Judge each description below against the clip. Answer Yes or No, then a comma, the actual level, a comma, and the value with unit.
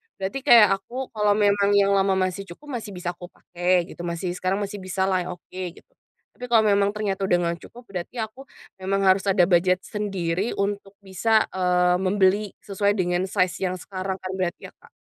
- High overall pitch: Yes, high, 195 Hz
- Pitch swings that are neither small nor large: No, narrow, 2.0 semitones